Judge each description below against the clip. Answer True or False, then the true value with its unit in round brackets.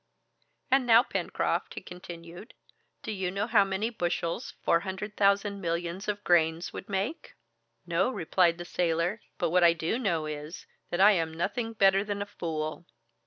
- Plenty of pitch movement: False (3.4 semitones)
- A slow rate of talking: False (165 wpm)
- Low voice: False (185 Hz)